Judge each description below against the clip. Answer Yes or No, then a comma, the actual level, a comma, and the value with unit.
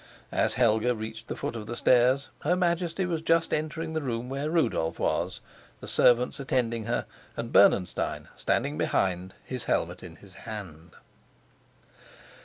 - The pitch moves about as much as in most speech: No, wide, 6.5 semitones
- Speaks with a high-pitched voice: No, low, 120 Hz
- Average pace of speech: Yes, average, 150 wpm